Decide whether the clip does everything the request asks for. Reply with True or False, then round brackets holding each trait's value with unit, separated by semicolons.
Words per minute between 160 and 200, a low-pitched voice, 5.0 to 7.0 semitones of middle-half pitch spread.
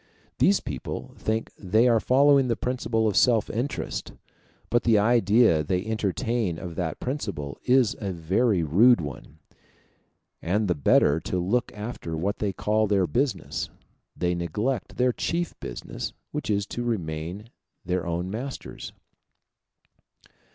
False (135 wpm; 105 Hz; 5.4 semitones)